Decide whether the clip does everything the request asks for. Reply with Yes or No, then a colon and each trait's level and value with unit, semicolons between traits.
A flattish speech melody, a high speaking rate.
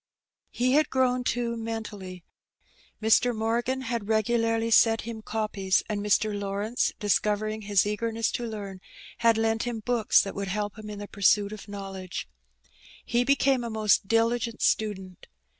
No: narrow, 2.3 semitones; average, 155 wpm